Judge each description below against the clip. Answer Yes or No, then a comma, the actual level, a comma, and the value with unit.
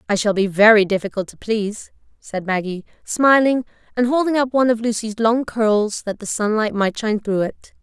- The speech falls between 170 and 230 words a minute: Yes, average, 190 wpm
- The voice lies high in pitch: Yes, high, 220 Hz